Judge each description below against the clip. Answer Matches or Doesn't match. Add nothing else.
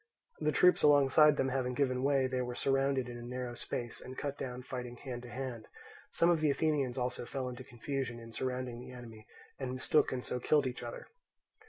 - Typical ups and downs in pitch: Doesn't match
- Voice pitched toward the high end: Doesn't match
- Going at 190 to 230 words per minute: Matches